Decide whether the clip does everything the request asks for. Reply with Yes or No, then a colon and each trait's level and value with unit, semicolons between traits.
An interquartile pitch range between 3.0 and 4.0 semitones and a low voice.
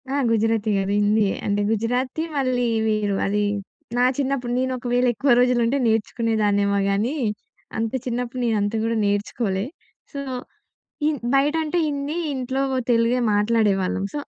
No: average, 3.6 semitones; high, 230 Hz